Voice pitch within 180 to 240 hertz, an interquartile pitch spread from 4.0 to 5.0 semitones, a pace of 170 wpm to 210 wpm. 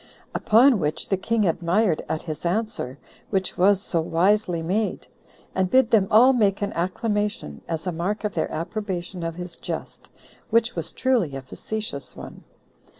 No: high, 190 Hz; average, 4.4 semitones; average, 160 wpm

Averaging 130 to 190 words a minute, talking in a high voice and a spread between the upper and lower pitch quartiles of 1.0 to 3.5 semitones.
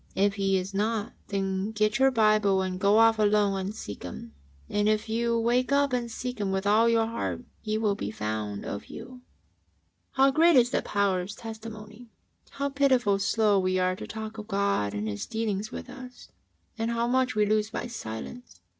No: average, 200 wpm; high, 215 Hz; average, 3.1 semitones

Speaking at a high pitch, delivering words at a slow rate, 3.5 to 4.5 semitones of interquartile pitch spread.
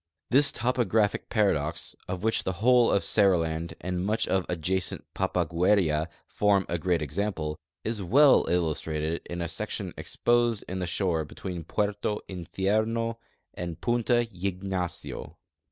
No: very low, 95 Hz; slow, 130 wpm; average, 4.1 semitones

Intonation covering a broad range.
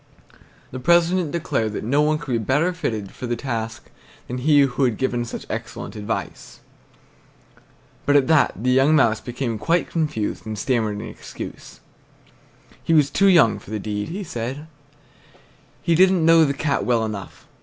Yes: wide, 5.7 semitones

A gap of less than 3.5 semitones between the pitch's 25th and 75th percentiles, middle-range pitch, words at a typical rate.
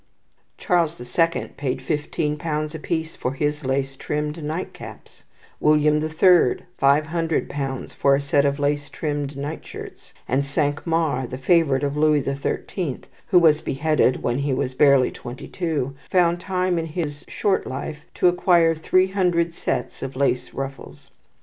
Yes: average, 3.1 semitones; medium, 150 Hz; average, 165 wpm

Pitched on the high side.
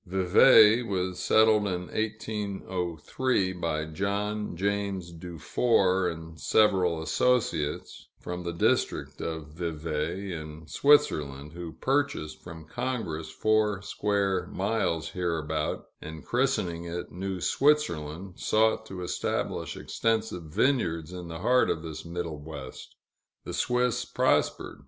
No: very low, 90 Hz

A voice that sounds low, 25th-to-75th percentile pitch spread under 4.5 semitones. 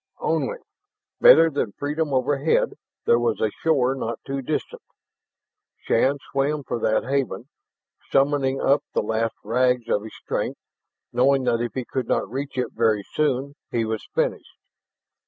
Yes: low, 130 Hz; average, 3.2 semitones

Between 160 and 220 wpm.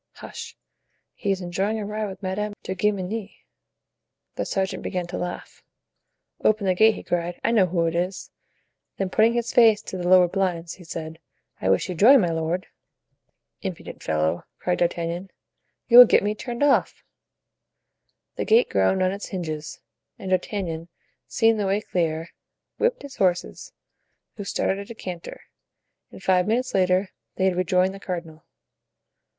Yes: average, 165 wpm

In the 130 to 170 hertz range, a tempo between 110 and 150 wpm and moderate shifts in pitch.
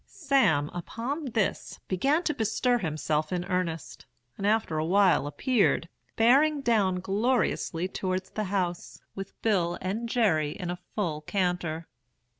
No: high, 190 Hz; slow, 135 wpm; average, 5.0 semitones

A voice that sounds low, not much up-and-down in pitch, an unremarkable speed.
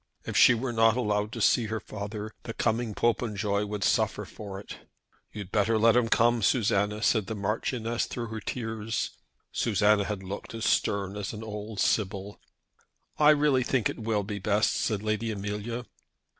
Yes: low, 110 Hz; narrow, 1.9 semitones; average, 170 wpm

